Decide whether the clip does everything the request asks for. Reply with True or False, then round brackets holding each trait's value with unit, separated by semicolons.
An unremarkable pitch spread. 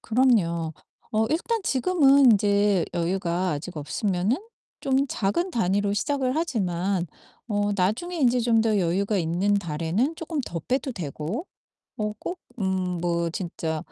False (6.5 semitones)